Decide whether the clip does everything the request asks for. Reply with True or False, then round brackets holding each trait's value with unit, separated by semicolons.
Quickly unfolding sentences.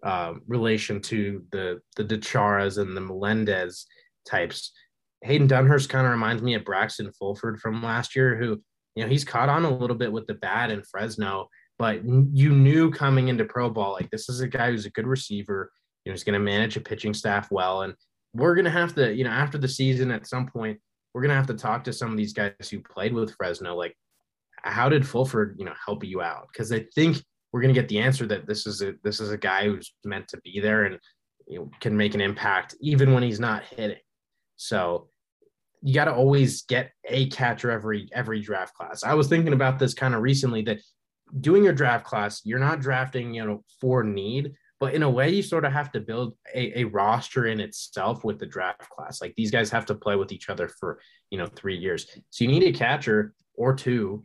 True (230 wpm)